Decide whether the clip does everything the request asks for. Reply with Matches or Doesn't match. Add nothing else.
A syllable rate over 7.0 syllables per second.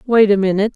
Matches